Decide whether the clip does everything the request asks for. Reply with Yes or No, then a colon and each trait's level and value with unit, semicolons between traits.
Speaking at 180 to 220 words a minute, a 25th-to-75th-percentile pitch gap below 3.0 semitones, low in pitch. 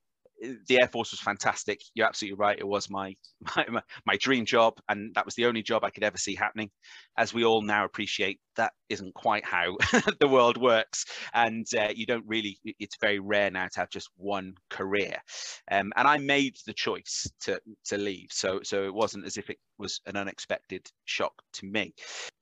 Yes: average, 200 wpm; narrow, 2.5 semitones; low, 105 Hz